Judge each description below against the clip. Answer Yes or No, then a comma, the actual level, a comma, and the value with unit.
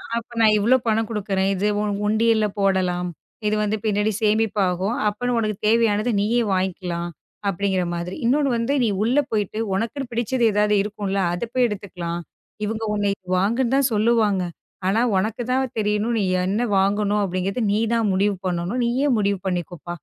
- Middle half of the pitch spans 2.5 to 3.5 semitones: Yes, average, 3.0 semitones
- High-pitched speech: Yes, high, 210 Hz